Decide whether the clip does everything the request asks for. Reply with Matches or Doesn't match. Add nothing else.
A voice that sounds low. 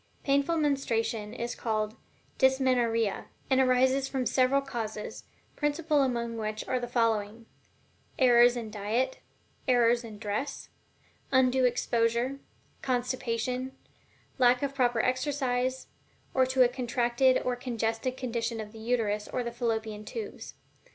Doesn't match